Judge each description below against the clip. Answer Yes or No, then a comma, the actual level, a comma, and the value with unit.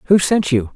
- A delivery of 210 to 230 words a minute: No, fast, 240 wpm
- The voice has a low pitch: No, medium, 155 Hz